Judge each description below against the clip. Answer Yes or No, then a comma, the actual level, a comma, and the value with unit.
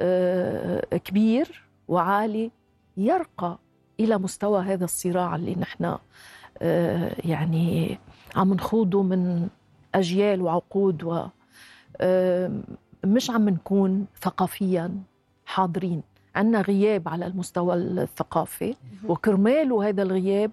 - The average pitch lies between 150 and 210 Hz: Yes, high, 190 Hz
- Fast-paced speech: No, average, 80 wpm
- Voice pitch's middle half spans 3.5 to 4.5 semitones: No, narrow, 2.6 semitones